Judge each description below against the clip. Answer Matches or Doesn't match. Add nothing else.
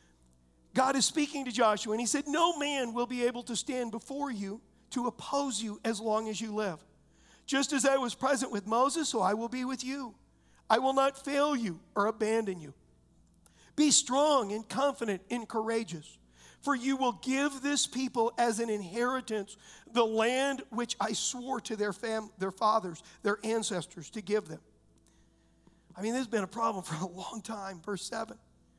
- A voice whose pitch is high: Matches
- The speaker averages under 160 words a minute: Doesn't match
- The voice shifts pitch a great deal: Doesn't match